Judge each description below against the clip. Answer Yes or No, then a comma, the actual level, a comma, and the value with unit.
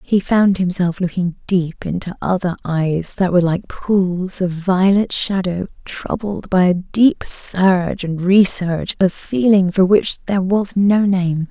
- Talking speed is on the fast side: No, average, 155 wpm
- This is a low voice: No, medium, 185 Hz